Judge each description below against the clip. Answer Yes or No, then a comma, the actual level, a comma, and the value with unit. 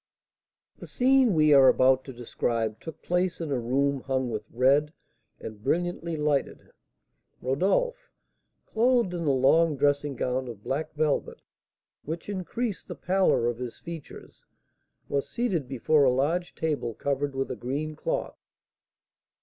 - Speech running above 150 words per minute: No, average, 140 wpm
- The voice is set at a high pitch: No, medium, 145 Hz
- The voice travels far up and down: No, average, 4.6 semitones